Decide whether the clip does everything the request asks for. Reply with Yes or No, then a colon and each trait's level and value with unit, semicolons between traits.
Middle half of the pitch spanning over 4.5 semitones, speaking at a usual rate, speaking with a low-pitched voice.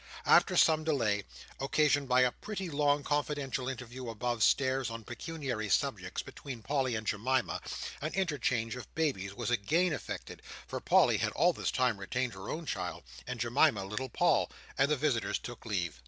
No: average, 4.2 semitones; average, 160 wpm; low, 130 Hz